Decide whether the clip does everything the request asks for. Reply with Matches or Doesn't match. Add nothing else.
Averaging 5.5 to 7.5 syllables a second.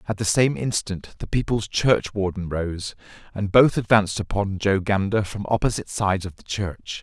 Doesn't match